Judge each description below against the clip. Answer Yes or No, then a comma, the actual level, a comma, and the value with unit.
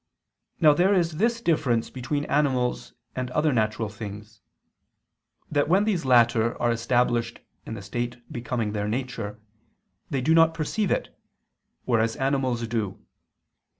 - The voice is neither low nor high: No, low, 125 Hz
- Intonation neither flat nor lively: Yes, average, 4.8 semitones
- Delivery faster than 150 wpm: No, slow, 135 wpm